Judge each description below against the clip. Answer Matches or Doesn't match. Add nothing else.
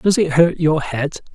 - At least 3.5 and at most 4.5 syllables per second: Matches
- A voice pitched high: Doesn't match